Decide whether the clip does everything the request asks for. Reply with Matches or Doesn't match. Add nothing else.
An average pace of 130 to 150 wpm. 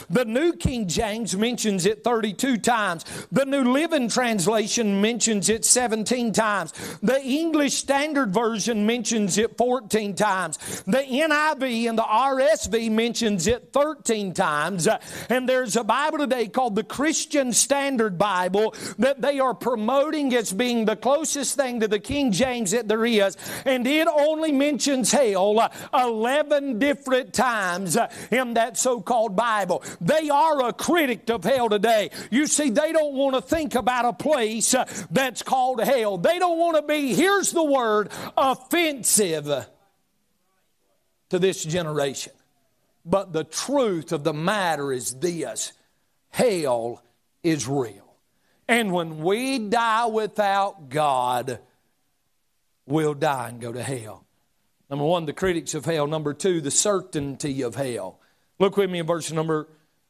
Matches